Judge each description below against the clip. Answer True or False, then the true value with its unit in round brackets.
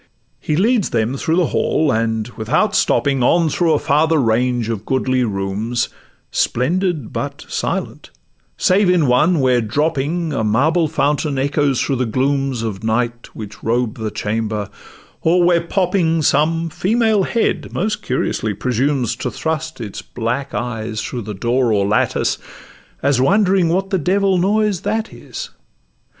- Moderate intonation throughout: False (6.6 semitones)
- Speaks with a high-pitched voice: False (140 Hz)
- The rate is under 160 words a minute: True (150 wpm)